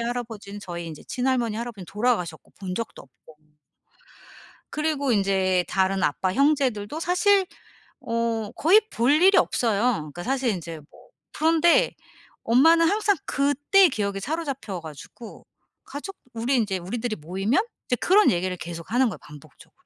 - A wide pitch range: Yes, wide, 7.2 semitones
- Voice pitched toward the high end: Yes, high, 230 Hz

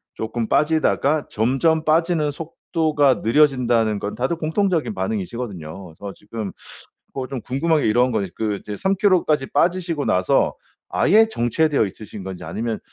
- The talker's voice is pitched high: No, low, 135 Hz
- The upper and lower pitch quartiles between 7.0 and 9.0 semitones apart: No, wide, 6.4 semitones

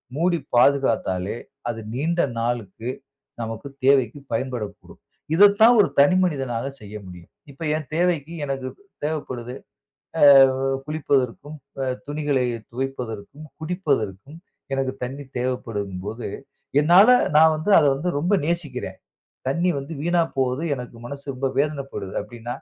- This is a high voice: No, low, 135 Hz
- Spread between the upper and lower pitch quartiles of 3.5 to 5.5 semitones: Yes, average, 4.6 semitones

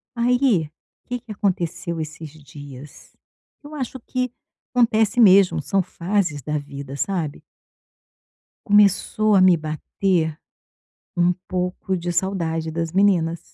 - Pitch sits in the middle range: Yes, medium, 180 Hz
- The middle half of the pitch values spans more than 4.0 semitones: Yes, average, 4.5 semitones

